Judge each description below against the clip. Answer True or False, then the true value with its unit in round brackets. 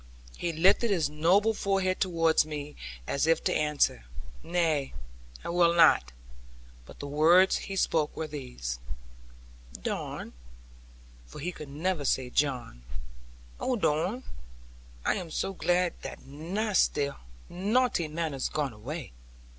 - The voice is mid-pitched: True (160 Hz)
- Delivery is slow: True (130 wpm)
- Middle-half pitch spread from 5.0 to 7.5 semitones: False (4.1 semitones)